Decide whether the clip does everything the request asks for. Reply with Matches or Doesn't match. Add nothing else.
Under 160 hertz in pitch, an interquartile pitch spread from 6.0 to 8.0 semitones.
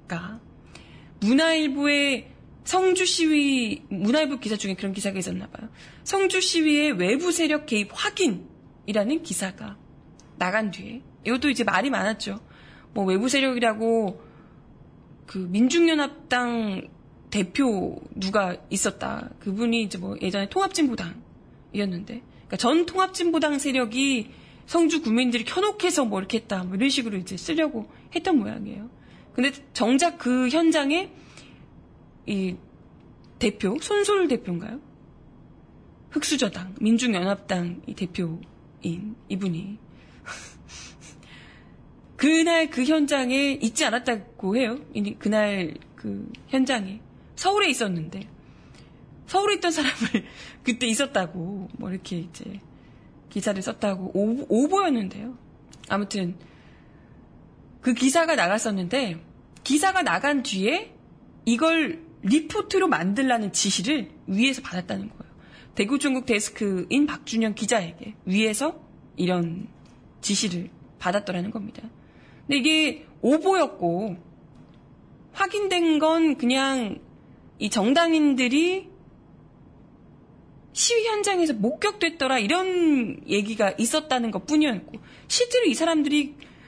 Doesn't match